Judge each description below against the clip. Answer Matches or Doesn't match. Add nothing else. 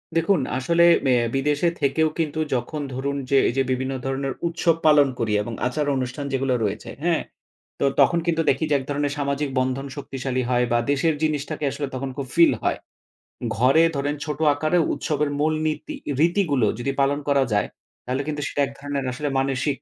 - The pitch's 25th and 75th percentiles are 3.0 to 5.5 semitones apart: Doesn't match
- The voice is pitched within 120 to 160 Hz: Matches